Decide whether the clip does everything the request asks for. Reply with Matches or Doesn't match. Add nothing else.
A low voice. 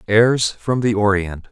Matches